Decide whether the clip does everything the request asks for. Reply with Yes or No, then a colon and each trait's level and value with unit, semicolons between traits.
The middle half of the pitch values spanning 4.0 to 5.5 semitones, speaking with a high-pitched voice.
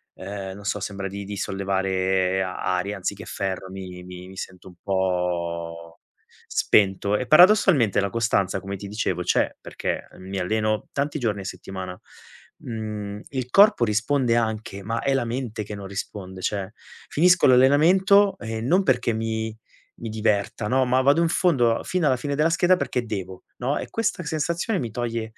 No: average, 5.2 semitones; low, 105 Hz